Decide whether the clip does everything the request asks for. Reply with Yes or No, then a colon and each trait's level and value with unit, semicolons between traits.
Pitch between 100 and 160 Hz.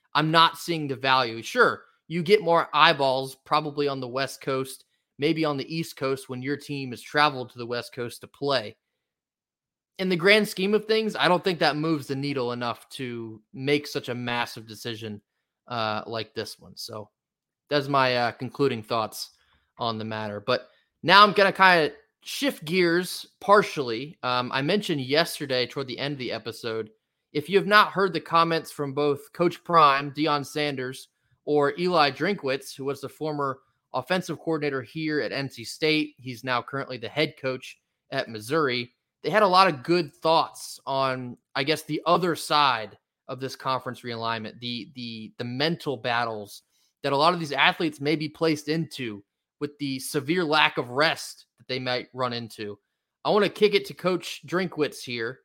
Yes: medium, 140 Hz